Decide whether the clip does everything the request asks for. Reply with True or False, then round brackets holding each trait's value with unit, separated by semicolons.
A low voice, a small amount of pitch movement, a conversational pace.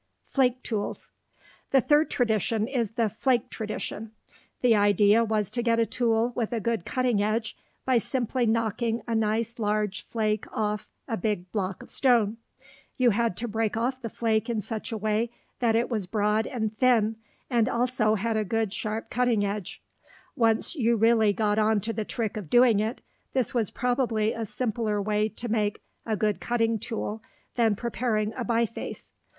False (225 Hz; 1.9 semitones; 175 wpm)